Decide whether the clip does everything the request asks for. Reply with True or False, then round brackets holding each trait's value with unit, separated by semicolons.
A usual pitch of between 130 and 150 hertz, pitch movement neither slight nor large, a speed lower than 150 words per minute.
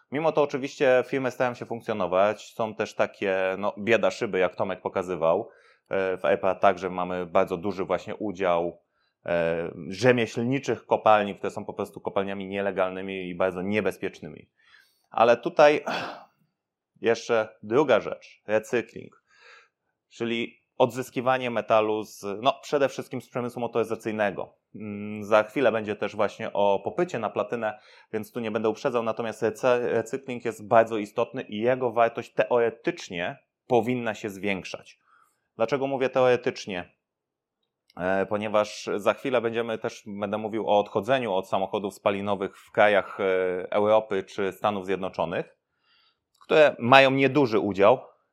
False (110 Hz; 3.5 semitones; 125 wpm)